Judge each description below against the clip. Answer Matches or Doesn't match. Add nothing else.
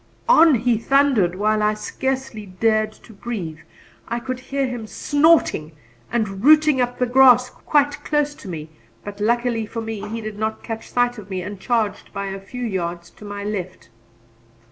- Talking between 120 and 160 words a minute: Doesn't match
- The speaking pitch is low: Doesn't match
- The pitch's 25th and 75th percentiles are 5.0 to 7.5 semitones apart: Doesn't match